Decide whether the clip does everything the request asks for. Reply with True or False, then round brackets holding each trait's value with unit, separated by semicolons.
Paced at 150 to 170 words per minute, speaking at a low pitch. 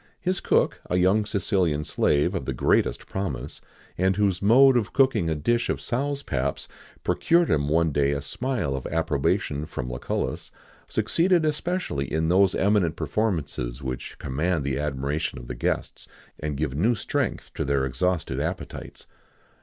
True (155 wpm; 85 Hz)